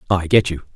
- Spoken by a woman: No, male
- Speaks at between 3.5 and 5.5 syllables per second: No, 6.3 syllables/s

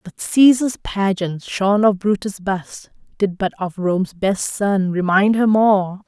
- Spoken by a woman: Yes, female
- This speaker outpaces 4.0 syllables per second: No, 3.8 syllables/s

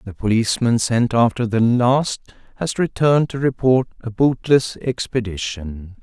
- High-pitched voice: No, low, 120 Hz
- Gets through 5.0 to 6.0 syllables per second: No, 4.5 syllables/s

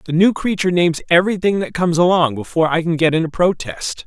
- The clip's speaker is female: No, male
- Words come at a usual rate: No, fast, 220 wpm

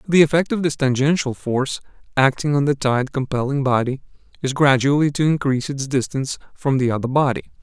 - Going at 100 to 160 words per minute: No, average, 175 wpm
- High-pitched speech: No, low, 135 Hz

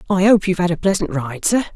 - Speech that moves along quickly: Yes, fast, 275 wpm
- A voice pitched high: No, medium, 180 Hz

